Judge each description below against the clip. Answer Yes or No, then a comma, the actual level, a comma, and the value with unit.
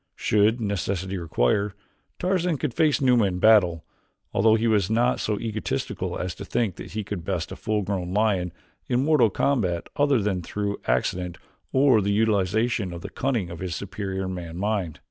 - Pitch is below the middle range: Yes, low, 100 Hz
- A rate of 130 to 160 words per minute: No, average, 175 wpm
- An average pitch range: Yes, average, 3.7 semitones